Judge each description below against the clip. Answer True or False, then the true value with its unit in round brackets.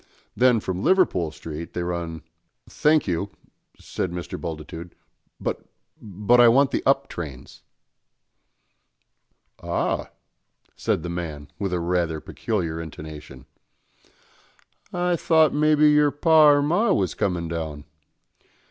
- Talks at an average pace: False (120 wpm)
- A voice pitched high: False (90 Hz)